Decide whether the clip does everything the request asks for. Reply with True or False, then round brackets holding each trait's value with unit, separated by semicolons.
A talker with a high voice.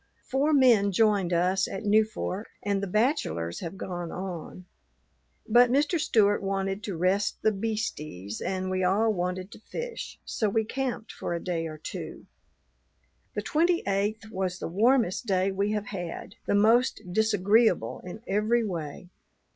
True (200 Hz)